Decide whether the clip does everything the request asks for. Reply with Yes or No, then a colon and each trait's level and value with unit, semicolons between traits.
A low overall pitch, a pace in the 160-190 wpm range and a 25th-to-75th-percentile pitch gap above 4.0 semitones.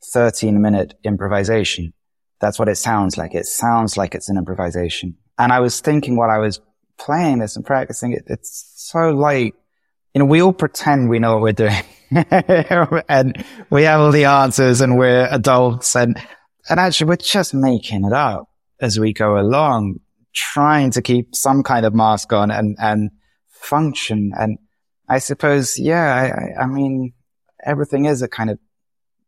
Yes: low, 125 Hz; average, 170 wpm; average, 5.2 semitones